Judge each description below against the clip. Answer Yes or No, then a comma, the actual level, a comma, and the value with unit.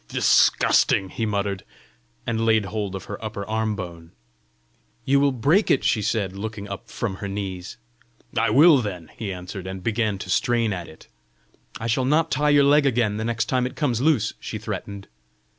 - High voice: No, low, 110 Hz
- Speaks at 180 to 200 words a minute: Yes, average, 185 wpm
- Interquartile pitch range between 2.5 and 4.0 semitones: Yes, average, 3.7 semitones